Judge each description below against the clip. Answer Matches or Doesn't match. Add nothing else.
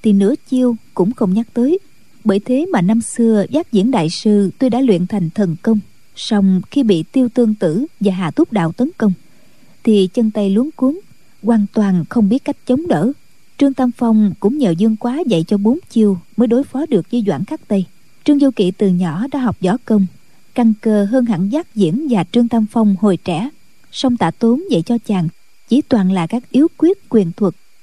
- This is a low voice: Doesn't match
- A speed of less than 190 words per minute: Doesn't match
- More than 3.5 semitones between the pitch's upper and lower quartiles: Matches